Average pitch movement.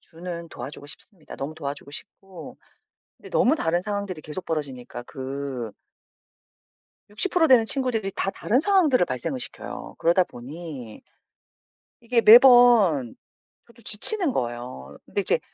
No: wide, 9.0 semitones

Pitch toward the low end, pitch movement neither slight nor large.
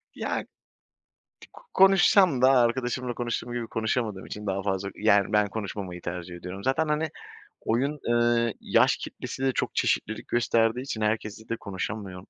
Yes: low, 115 Hz; average, 3.8 semitones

